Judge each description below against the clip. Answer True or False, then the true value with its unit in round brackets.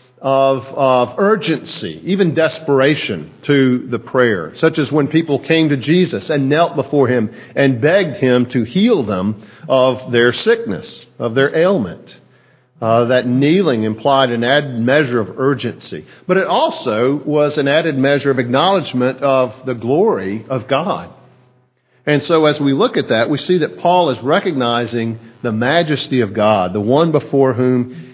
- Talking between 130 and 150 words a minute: False (160 wpm)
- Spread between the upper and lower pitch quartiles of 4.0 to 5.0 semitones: False (3.4 semitones)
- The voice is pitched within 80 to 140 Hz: True (135 Hz)